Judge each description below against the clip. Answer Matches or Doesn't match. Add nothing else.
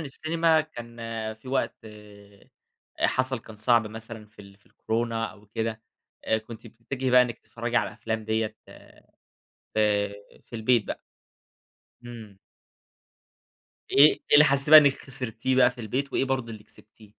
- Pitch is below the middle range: Matches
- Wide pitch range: Doesn't match